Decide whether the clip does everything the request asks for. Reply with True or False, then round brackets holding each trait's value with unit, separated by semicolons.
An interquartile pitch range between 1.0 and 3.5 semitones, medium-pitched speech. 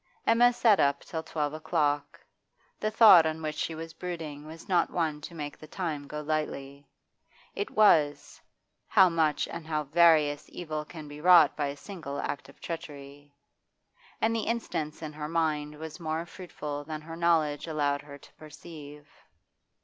True (2.4 semitones; 155 Hz)